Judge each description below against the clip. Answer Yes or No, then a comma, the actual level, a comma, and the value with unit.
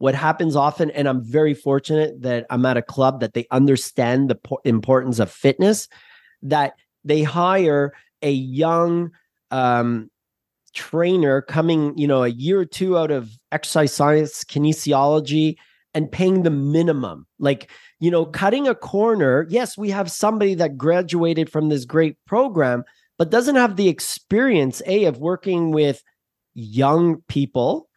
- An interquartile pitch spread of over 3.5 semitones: Yes, average, 4.2 semitones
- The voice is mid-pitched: Yes, medium, 155 Hz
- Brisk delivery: No, average, 150 wpm